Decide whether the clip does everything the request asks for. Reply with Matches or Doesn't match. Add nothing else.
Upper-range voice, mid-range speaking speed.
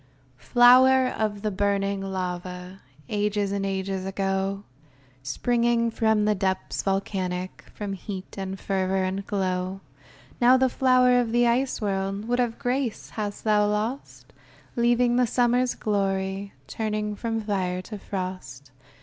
Doesn't match